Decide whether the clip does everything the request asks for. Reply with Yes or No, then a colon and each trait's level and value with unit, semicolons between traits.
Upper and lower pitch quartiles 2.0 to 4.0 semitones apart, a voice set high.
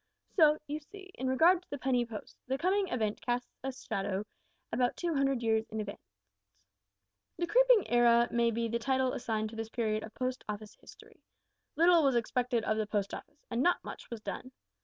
No: average, 4.7 semitones; high, 245 Hz